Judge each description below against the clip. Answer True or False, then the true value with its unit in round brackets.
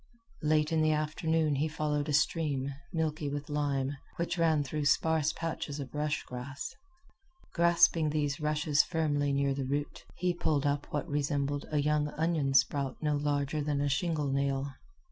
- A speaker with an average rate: True (165 wpm)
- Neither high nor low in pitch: True (150 Hz)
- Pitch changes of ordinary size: False (1.7 semitones)